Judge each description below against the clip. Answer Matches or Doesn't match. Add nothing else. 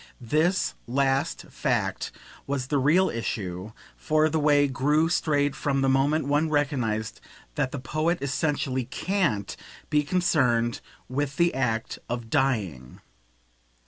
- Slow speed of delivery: Matches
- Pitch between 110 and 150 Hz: Matches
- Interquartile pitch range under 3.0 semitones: Doesn't match